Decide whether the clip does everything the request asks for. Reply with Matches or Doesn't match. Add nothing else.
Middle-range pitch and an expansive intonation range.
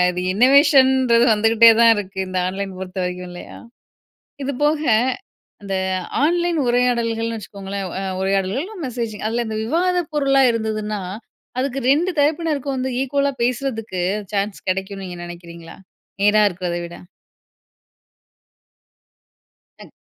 Doesn't match